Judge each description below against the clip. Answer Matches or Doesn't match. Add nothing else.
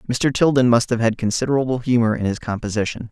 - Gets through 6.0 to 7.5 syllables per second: Matches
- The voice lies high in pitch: Doesn't match